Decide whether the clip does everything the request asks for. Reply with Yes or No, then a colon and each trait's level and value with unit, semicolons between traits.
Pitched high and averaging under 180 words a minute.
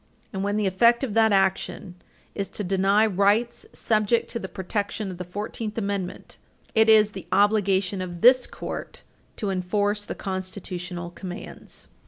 Yes: high, 200 Hz; average, 155 wpm